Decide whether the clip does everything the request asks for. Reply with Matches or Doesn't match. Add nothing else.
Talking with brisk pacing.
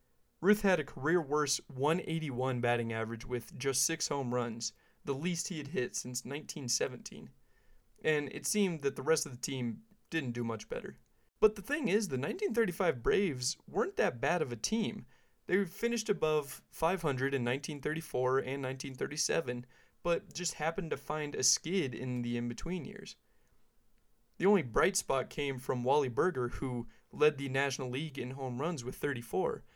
Doesn't match